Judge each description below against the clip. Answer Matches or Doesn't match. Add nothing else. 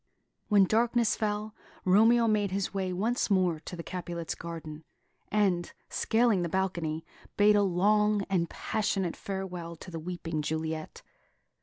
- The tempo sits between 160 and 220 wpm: Doesn't match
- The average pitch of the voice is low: Doesn't match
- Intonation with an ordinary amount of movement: Matches